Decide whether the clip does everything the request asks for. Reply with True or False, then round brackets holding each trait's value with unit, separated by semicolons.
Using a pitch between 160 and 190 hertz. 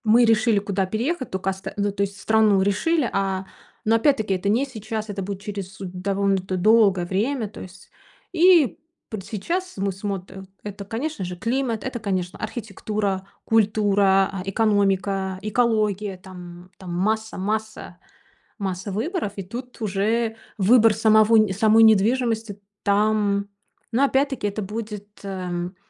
False (205 Hz)